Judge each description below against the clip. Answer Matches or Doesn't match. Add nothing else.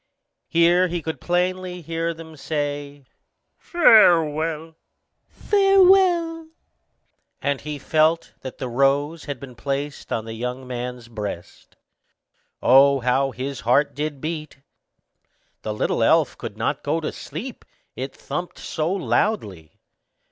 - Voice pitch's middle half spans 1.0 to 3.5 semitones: Doesn't match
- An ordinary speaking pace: Doesn't match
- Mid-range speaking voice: Matches